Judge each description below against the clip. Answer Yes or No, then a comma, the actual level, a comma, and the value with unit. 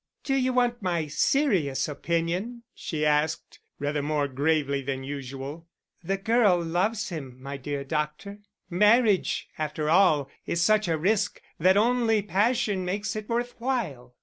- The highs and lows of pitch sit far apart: Yes, wide, 6.4 semitones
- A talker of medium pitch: Yes, medium, 175 Hz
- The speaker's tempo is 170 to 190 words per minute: No, average, 145 wpm